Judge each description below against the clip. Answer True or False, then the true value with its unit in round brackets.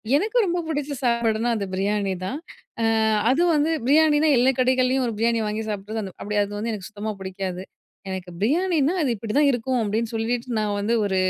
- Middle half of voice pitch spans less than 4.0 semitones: False (4.5 semitones)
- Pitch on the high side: True (230 Hz)